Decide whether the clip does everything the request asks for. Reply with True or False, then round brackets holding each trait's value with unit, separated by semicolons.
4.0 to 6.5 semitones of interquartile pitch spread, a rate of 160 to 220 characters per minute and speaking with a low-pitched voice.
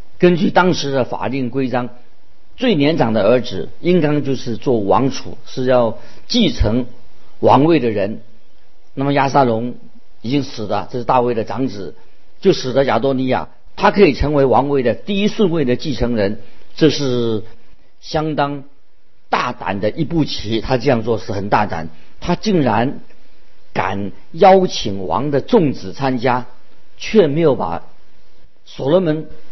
True (5.1 semitones; 215 characters per minute; 130 Hz)